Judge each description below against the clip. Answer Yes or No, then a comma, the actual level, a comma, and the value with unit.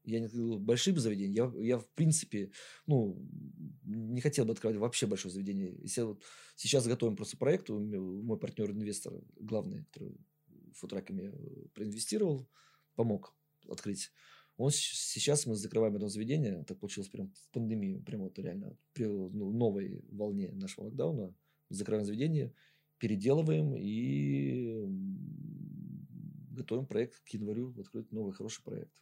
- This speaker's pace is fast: No, average, 135 wpm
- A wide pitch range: Yes, wide, 6.8 semitones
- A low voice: Yes, low, 120 Hz